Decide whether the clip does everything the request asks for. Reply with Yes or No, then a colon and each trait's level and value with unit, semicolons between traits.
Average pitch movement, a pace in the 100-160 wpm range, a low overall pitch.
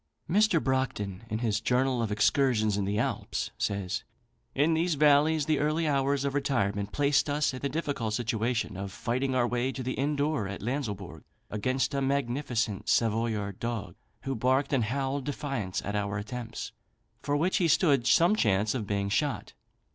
No: average, 4.9 semitones; average, 170 wpm; low, 130 Hz